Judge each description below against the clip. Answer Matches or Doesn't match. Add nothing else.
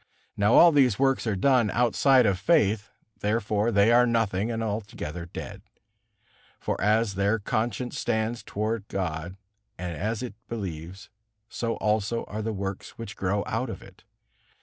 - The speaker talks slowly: Doesn't match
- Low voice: Matches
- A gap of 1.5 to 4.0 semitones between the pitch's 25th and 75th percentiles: Matches